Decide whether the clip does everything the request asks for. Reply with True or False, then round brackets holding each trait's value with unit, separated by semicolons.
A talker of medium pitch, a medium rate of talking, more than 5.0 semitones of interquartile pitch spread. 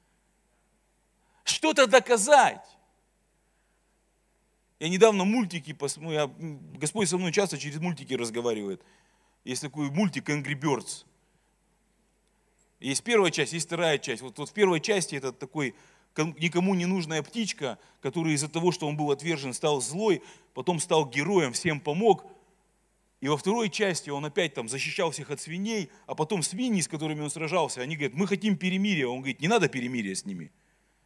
True (165 Hz; 150 wpm; 5.4 semitones)